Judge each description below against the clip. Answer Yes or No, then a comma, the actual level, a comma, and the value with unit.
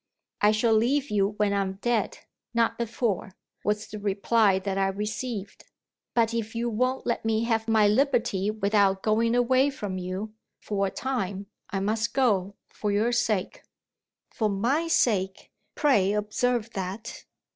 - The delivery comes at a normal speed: Yes, average, 150 wpm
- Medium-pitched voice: No, high, 215 Hz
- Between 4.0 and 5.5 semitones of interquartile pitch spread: No, average, 2.9 semitones